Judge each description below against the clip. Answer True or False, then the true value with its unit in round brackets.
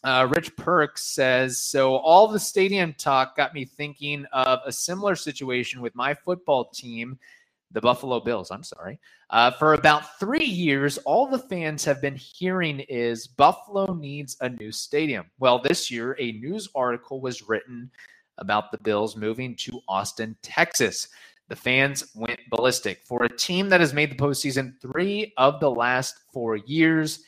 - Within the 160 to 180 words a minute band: True (165 wpm)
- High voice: False (135 Hz)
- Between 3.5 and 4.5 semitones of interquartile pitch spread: True (4.0 semitones)